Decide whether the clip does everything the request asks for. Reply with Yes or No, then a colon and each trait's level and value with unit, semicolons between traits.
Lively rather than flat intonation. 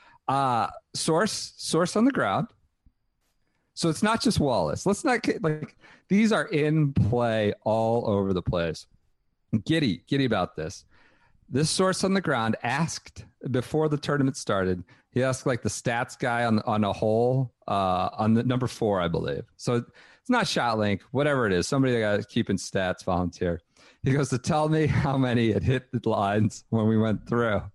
Yes: wide, 5.9 semitones